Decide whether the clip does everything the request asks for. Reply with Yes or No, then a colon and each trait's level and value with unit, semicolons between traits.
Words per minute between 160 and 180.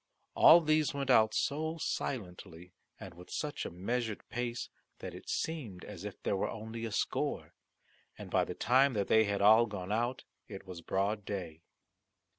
Yes: average, 175 wpm